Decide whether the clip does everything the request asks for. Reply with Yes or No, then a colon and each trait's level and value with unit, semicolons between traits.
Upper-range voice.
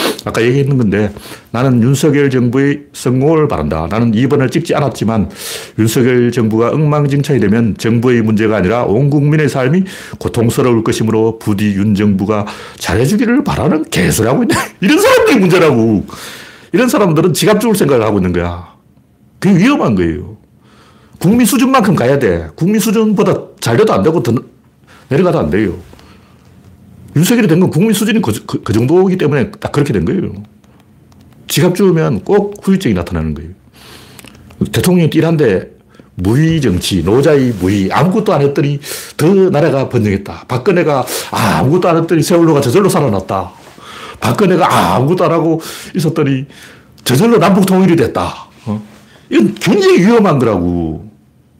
No: medium, 140 Hz